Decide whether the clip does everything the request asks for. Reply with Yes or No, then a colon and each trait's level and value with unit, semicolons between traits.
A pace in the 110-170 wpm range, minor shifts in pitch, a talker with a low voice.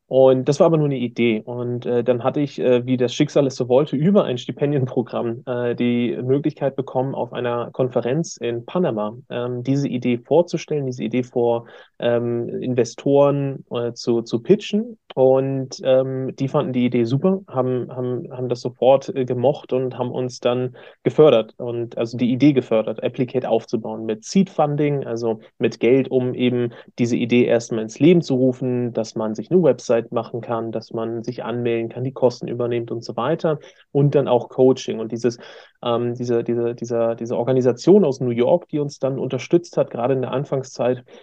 No: average, 185 wpm; narrow, 2.2 semitones; low, 125 Hz